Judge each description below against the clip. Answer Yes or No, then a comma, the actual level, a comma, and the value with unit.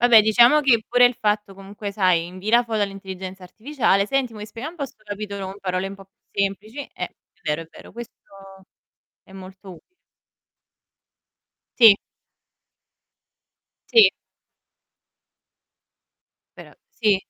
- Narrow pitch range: No, average, 3.5 semitones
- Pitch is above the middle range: Yes, high, 205 Hz